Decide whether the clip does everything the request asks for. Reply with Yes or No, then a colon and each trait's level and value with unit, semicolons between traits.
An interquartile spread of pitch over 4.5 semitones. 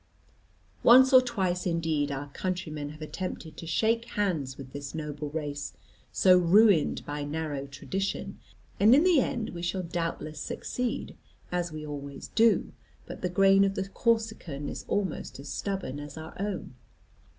Yes: average, 5.2 semitones